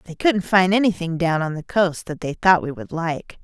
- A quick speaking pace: Yes, fast, 245 wpm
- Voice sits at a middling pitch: Yes, medium, 175 Hz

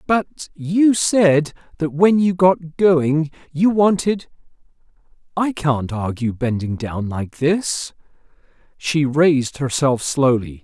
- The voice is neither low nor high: Yes, medium, 155 Hz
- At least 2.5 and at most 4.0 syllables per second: Yes, 3.4 syllables/s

